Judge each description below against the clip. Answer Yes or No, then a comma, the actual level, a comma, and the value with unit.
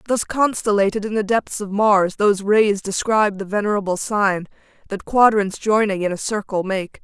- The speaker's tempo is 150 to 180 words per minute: Yes, average, 170 wpm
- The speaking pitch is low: No, high, 205 Hz